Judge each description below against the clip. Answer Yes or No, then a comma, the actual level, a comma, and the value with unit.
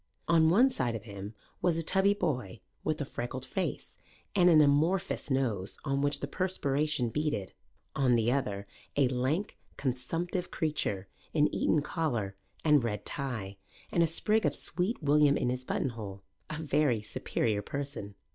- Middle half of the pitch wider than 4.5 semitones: Yes, average, 5.1 semitones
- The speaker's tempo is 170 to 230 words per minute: No, average, 155 wpm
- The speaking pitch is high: No, medium, 140 Hz